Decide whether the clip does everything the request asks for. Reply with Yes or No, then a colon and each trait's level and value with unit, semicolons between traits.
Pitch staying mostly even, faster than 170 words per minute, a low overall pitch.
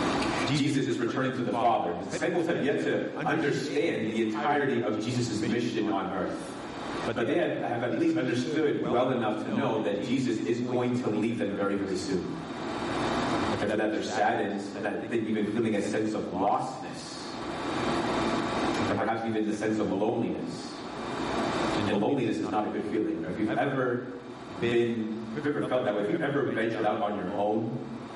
Yes: narrow, 2.2 semitones; average, 185 wpm; low, 110 Hz